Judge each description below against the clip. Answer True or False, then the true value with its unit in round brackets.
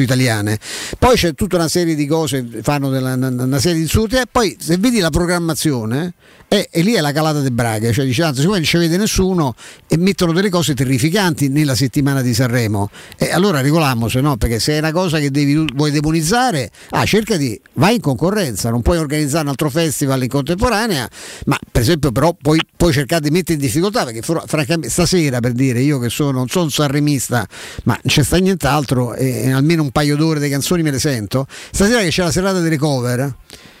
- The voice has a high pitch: False (150 Hz)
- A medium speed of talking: False (210 wpm)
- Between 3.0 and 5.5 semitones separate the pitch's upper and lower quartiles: True (4.5 semitones)